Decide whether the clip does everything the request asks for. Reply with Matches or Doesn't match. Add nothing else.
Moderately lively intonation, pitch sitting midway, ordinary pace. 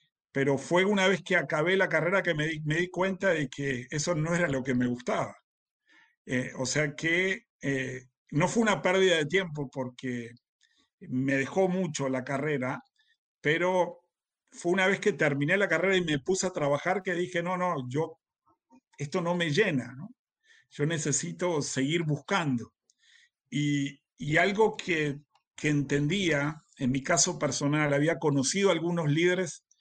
Matches